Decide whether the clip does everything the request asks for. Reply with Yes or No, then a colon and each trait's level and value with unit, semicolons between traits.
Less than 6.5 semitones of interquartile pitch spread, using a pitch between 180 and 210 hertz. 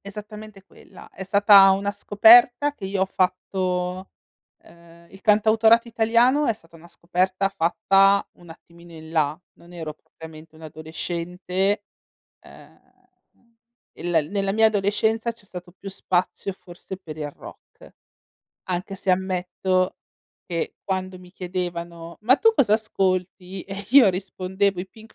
Yes: average, 2.7 semitones; high, 190 Hz